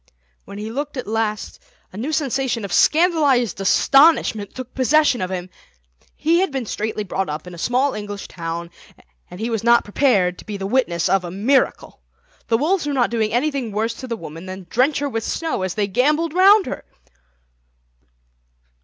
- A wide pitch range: Yes, wide, 6.0 semitones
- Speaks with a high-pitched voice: Yes, high, 230 Hz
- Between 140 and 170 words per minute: No, average, 185 wpm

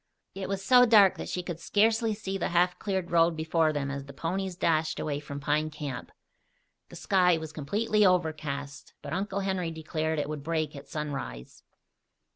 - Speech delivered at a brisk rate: No, average, 180 wpm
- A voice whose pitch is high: No, medium, 165 Hz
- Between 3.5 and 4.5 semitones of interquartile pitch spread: Yes, average, 4.2 semitones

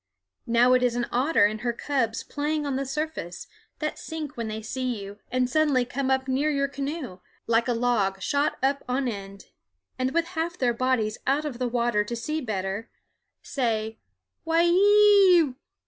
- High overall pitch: Yes, very high, 255 Hz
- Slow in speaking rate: No, average, 190 wpm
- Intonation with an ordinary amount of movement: Yes, average, 4.5 semitones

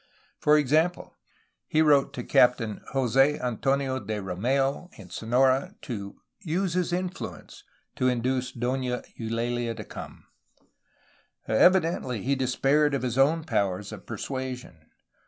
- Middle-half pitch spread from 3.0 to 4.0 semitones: Yes, average, 3.6 semitones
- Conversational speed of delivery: No, slow, 130 wpm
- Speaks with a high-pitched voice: No, low, 130 Hz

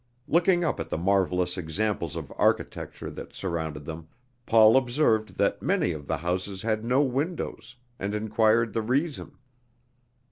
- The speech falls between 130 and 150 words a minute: Yes, average, 145 wpm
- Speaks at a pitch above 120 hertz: No, low, 110 Hz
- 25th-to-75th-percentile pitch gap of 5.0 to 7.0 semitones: Yes, wide, 5.6 semitones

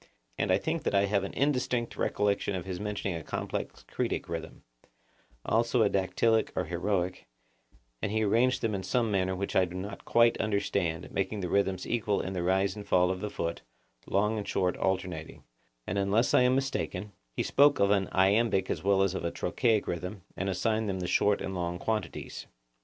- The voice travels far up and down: No, average, 2.8 semitones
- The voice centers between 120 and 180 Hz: No, low, 100 Hz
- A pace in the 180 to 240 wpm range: Yes, average, 195 wpm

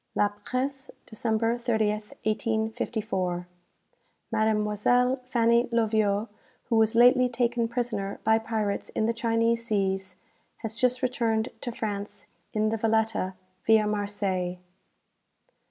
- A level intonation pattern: Yes, narrow, 2.0 semitones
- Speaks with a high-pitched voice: Yes, high, 220 Hz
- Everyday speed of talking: No, slow, 115 wpm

